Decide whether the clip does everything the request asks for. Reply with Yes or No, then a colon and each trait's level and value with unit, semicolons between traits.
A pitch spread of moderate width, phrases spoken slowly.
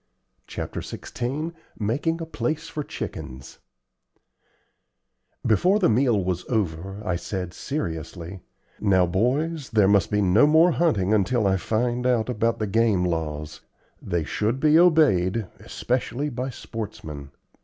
No: wide, 6.8 semitones; slow, 130 wpm